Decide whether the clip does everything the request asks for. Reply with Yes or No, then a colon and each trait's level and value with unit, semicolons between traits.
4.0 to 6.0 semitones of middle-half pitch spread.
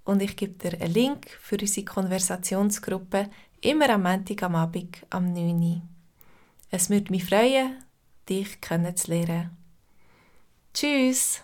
No: average, 2.7 semitones